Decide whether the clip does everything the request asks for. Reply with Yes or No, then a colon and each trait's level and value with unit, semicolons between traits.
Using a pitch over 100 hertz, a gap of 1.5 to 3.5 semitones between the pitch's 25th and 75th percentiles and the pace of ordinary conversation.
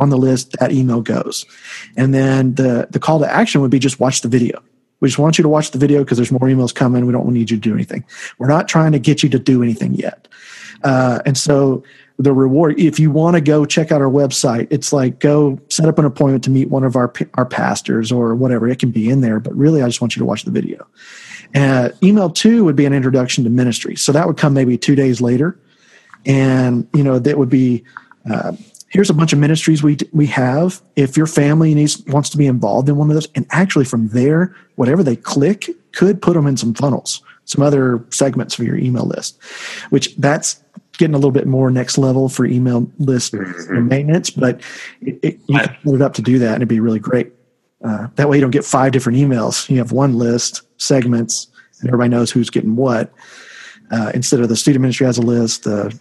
No: low, 135 Hz; average, 3.2 semitones; fast, 240 wpm